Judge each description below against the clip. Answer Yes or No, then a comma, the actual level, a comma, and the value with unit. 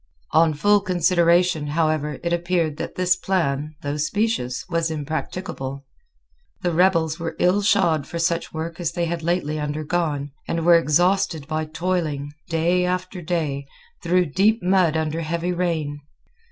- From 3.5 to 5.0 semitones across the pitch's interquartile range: No, average, 2.8 semitones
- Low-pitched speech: No, medium, 165 Hz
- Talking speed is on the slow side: No, average, 145 wpm